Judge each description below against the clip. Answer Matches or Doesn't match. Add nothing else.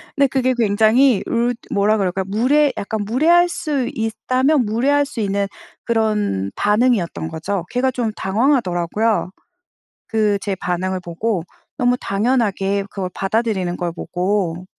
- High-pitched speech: Matches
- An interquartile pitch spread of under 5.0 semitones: Matches